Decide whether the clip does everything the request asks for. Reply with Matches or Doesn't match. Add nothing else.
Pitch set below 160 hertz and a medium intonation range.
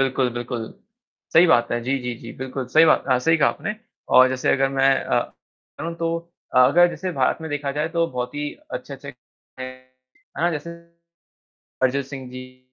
Matches